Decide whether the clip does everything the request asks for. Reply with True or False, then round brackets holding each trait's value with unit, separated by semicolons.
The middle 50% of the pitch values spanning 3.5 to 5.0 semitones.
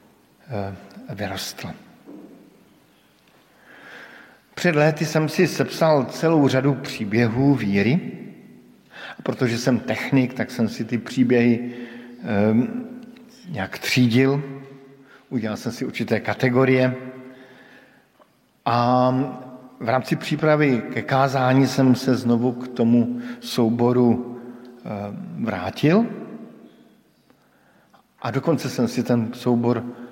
False (2.6 semitones)